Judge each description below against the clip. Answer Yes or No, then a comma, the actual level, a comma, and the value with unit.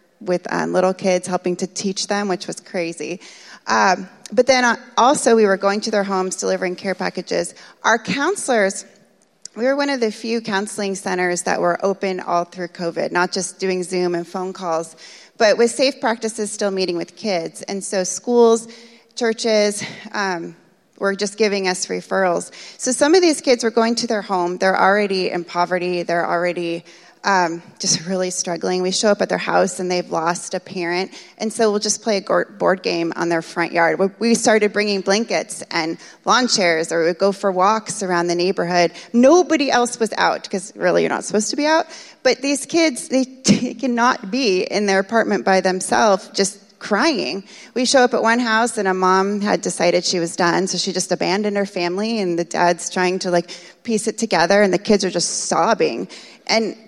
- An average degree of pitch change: Yes, average, 3.8 semitones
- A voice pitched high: Yes, high, 195 Hz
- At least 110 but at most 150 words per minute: No, average, 195 wpm